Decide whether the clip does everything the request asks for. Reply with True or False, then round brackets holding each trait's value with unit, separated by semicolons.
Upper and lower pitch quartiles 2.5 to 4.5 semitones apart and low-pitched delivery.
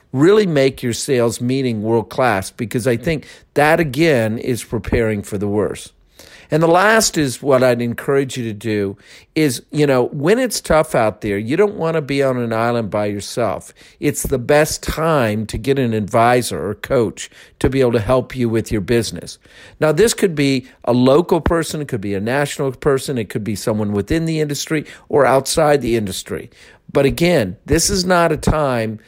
False (5.1 semitones; 130 Hz)